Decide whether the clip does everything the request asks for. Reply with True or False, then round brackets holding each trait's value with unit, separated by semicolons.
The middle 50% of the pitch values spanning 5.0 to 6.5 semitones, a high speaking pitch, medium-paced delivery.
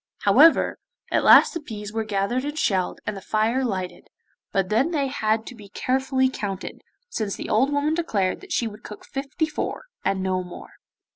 True (5.3 semitones; 220 Hz; 190 wpm)